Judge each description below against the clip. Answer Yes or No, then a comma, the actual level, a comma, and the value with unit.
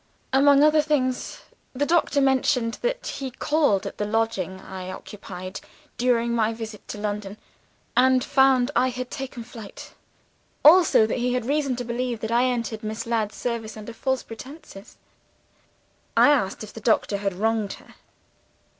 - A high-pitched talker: Yes, high, 235 Hz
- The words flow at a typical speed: Yes, average, 160 wpm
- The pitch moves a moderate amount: Yes, average, 3.7 semitones